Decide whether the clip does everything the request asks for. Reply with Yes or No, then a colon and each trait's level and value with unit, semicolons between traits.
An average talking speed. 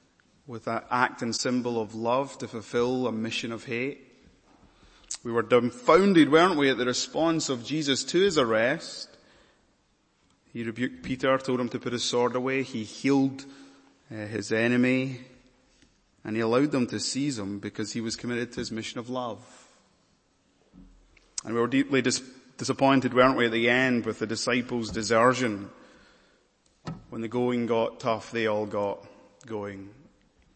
Yes: average, 160 wpm